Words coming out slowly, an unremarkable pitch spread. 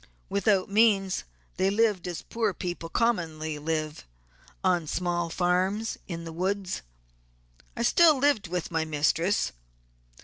Yes: slow, 125 wpm; average, 3.7 semitones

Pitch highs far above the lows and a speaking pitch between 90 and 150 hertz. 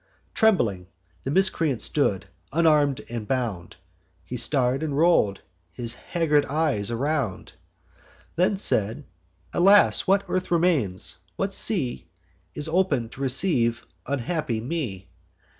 Yes: wide, 6.5 semitones; medium, 140 Hz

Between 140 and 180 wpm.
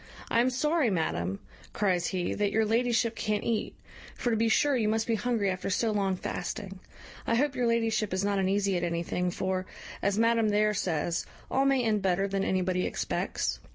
No: average, 190 wpm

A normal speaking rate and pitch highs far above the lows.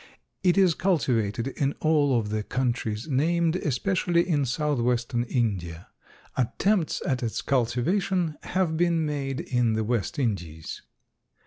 No: slow, 125 wpm; wide, 6.0 semitones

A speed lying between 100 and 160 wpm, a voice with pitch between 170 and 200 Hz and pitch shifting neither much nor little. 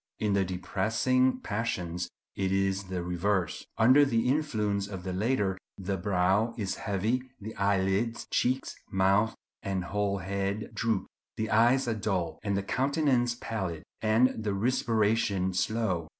No: slow, 135 wpm; low, 100 Hz; average, 3.1 semitones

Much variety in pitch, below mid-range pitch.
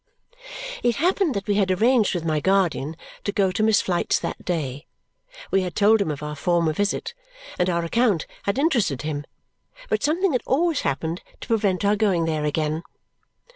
No: wide, 5.7 semitones; high, 190 Hz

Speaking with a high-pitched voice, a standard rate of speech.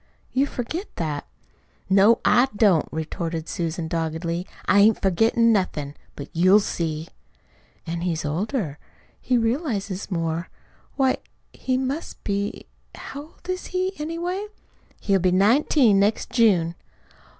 No: high, 200 Hz; slow, 125 wpm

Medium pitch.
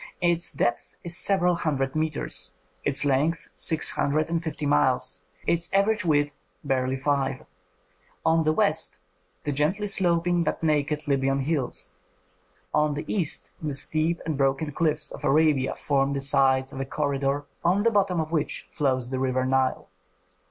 Yes: medium, 150 Hz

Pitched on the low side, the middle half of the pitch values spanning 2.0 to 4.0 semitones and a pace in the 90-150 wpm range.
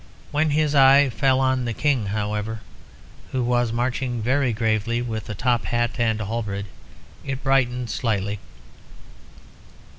Yes: low, 120 Hz; average, 3.3 semitones; average, 140 wpm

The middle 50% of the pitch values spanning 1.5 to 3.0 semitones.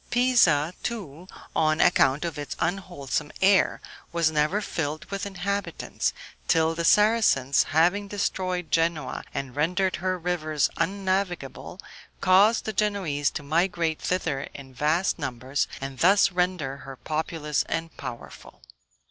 No: average, 4.3 semitones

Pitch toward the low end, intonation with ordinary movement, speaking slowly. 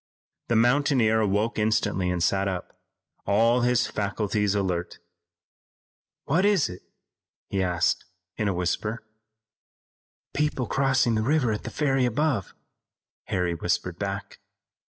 Yes: low, 110 Hz; average, 4.5 semitones; slow, 120 wpm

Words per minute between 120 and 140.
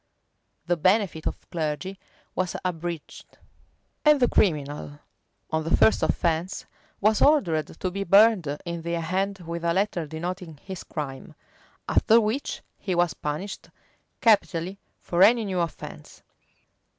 Yes: slow, 135 wpm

